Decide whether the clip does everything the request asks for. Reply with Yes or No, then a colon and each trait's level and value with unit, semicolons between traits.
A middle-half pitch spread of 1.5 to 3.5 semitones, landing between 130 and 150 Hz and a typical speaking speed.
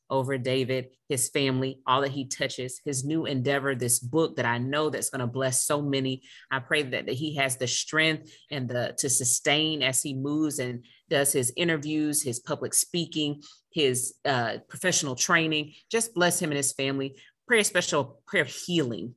Yes: average, 2.9 semitones; medium, 140 Hz; average, 190 wpm